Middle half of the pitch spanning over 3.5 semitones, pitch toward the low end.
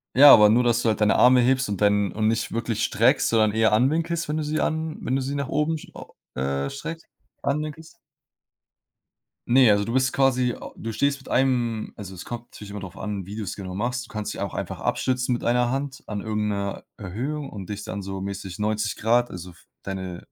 Yes: average, 4.5 semitones; low, 115 Hz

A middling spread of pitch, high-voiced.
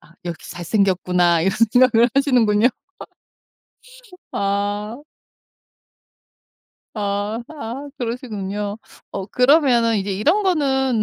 Yes: average, 4.2 semitones; high, 220 Hz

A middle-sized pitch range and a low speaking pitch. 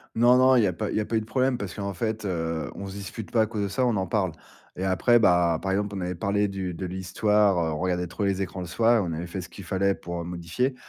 Yes: average, 3.4 semitones; very low, 95 Hz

